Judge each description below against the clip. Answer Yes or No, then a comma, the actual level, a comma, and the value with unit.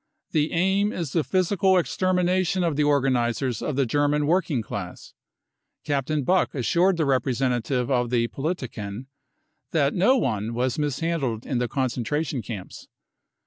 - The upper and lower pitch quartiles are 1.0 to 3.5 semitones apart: No, wide, 5.5 semitones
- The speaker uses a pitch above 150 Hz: No, medium, 145 Hz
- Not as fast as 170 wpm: Yes, average, 140 wpm